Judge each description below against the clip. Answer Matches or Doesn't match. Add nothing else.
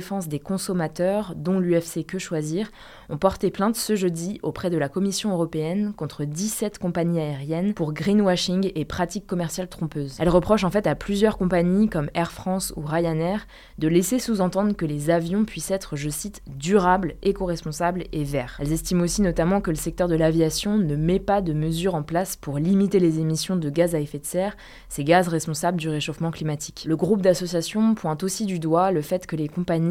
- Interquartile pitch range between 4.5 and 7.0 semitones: Doesn't match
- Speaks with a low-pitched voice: Doesn't match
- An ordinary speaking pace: Matches